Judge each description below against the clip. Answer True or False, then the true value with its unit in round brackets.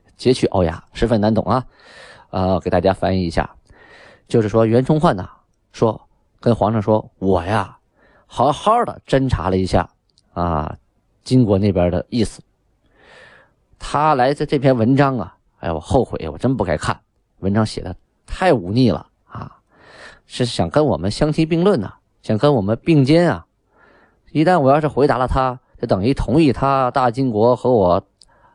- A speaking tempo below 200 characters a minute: False (240 characters per minute)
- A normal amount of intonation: False (5.7 semitones)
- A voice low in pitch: True (115 Hz)